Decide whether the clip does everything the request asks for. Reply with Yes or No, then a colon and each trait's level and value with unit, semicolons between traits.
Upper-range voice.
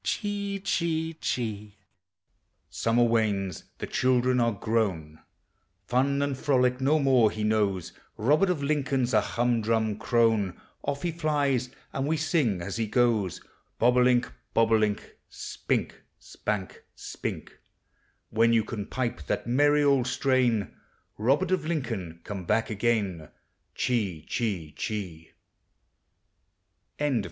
No: low, 120 Hz